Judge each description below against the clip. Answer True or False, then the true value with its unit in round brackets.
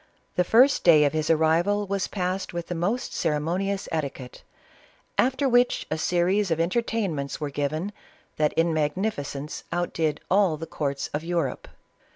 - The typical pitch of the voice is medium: True (170 Hz)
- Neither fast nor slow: True (155 wpm)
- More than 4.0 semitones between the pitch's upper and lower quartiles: True (4.4 semitones)